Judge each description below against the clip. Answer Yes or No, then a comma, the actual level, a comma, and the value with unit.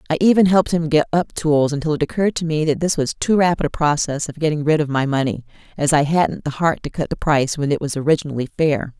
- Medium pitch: Yes, medium, 155 Hz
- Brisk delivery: Yes, fast, 260 wpm